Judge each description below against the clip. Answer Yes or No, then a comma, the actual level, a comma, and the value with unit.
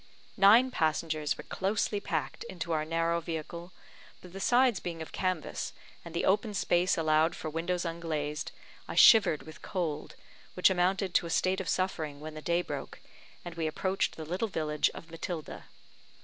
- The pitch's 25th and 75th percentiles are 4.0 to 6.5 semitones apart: No, average, 3.0 semitones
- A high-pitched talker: No, medium, 170 Hz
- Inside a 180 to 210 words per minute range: No, average, 170 wpm